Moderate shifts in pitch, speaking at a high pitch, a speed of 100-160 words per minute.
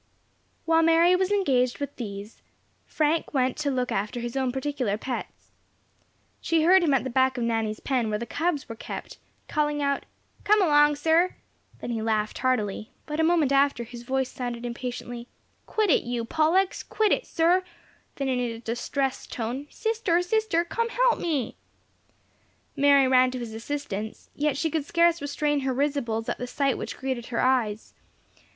No: average, 5.0 semitones; very high, 270 Hz; average, 170 wpm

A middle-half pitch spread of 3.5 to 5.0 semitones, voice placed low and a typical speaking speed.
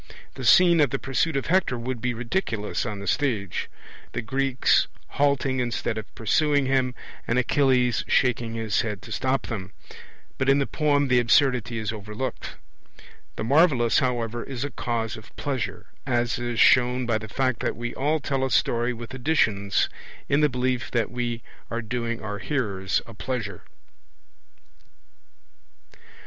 No: average, 2.9 semitones; low, 125 Hz; average, 160 wpm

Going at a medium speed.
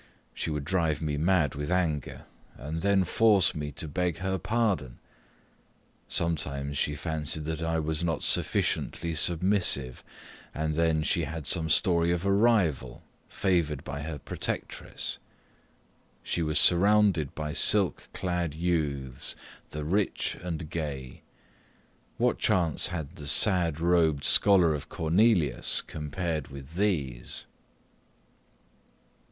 No: slow, 125 wpm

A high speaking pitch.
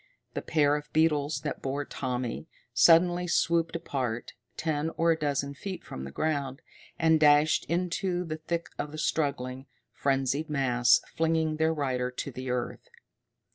No: medium, 150 Hz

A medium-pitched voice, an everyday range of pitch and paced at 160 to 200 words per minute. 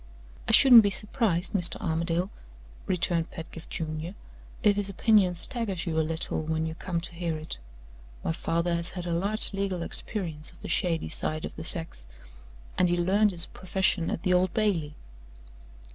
Yes: medium, 175 Hz; average, 3.0 semitones; average, 175 wpm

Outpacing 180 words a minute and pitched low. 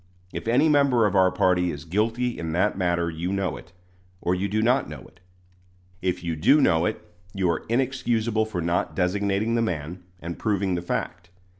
Yes: average, 190 wpm; very low, 95 Hz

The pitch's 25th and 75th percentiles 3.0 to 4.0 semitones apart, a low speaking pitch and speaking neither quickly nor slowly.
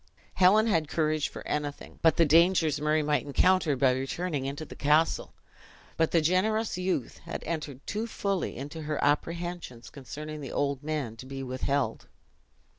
No: average, 3.5 semitones; medium, 155 Hz; average, 160 wpm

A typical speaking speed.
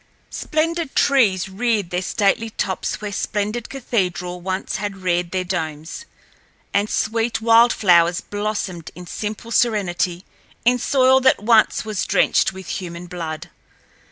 No: slow, 130 wpm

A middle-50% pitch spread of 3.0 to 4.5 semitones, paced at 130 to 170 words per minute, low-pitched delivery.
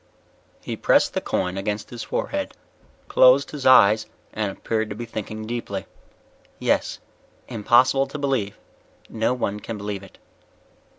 Yes: average, 3.8 semitones; slow, 135 wpm; low, 110 Hz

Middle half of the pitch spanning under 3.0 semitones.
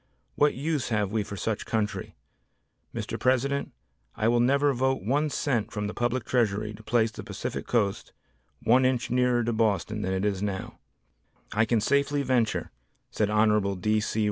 No: average, 3.5 semitones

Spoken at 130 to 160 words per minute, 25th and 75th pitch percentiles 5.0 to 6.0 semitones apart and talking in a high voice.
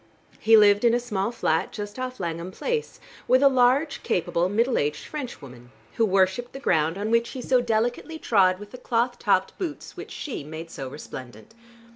No: average, 185 wpm; average, 5.3 semitones; high, 220 Hz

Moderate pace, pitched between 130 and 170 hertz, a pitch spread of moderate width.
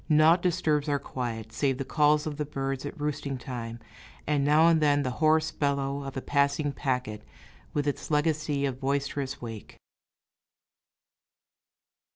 No: average, 150 wpm; medium, 140 Hz; narrow, 2.0 semitones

